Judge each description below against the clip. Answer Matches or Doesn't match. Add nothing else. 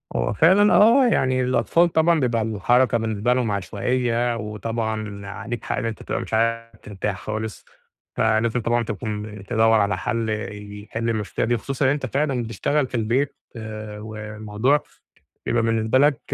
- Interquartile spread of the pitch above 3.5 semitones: Doesn't match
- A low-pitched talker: Matches